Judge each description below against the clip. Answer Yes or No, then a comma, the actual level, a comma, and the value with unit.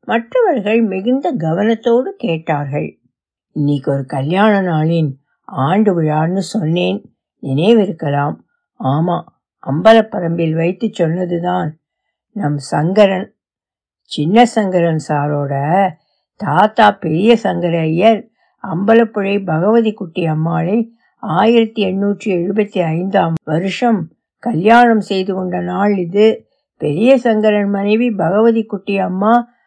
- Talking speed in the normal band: Yes, average, 90 wpm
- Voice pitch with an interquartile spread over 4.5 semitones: Yes, average, 5.2 semitones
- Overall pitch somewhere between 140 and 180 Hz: No, high, 190 Hz